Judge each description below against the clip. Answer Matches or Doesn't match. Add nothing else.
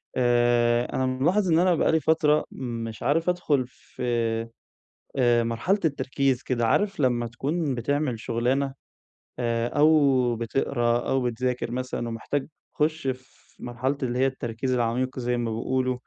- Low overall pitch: Matches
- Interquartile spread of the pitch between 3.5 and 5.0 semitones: Doesn't match